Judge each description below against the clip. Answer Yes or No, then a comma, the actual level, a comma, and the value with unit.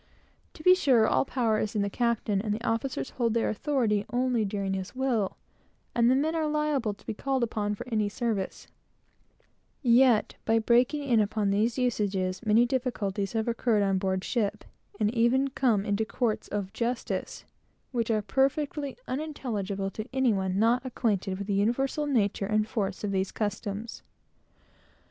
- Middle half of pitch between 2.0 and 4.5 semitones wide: Yes, average, 3.8 semitones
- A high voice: Yes, high, 225 Hz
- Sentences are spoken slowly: No, average, 165 wpm